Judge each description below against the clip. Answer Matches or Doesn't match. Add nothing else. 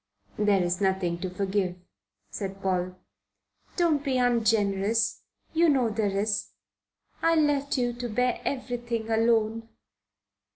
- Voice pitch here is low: Doesn't match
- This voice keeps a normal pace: Doesn't match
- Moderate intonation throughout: Matches